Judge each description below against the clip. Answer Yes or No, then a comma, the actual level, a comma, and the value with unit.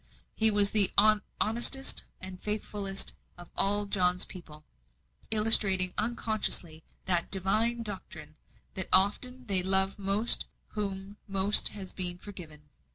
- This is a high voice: Yes, high, 195 Hz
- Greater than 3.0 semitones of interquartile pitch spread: No, narrow, 2.5 semitones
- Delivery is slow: Yes, slow, 120 wpm